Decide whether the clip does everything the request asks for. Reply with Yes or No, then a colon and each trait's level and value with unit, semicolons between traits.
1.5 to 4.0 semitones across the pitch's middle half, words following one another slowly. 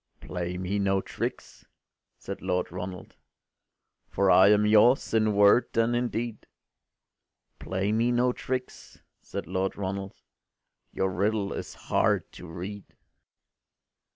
Yes: average, 2.9 semitones; slow, 125 wpm